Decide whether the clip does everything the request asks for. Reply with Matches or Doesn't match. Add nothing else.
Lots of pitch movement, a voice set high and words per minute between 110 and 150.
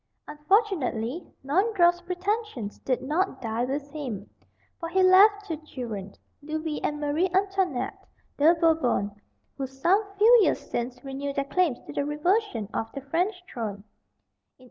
Matches